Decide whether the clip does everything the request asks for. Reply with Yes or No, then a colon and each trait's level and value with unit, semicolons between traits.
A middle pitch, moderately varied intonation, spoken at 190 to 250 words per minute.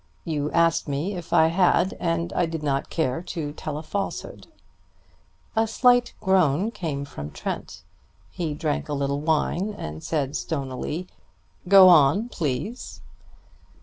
No: medium, 160 Hz; average, 4.3 semitones; average, 140 wpm